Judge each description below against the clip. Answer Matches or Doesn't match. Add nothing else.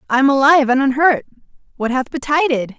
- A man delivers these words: Doesn't match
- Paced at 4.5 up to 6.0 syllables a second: Doesn't match